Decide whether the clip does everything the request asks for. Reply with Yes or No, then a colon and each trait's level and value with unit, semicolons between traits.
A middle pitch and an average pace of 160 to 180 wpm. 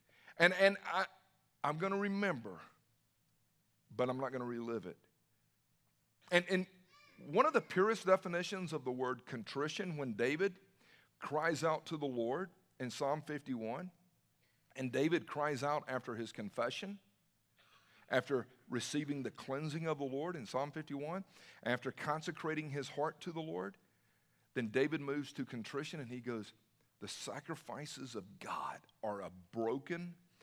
No: medium, 150 Hz; average, 145 wpm